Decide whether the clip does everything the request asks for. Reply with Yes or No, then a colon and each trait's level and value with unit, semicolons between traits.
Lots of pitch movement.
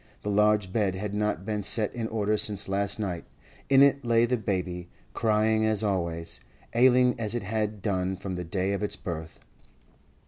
No: average, 2.7 semitones